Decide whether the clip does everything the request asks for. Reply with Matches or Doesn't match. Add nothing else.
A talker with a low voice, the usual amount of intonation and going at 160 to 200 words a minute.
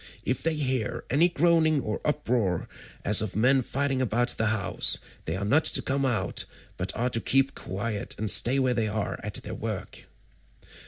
Matches